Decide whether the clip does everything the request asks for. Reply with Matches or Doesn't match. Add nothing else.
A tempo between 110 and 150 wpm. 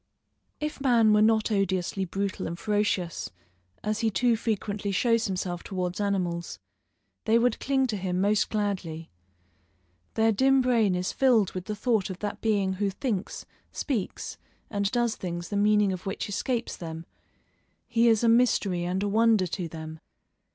Doesn't match